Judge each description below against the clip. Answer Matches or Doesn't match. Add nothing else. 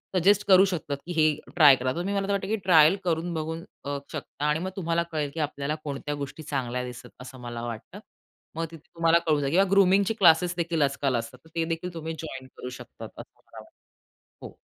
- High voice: Doesn't match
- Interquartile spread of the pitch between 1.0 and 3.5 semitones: Doesn't match